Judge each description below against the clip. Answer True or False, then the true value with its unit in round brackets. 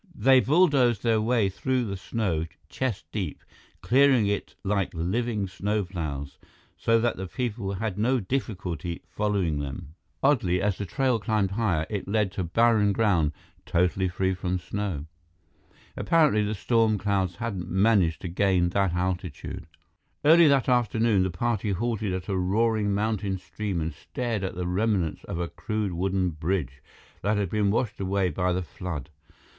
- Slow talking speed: False (155 wpm)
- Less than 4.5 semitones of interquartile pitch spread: True (3.8 semitones)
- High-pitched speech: False (100 Hz)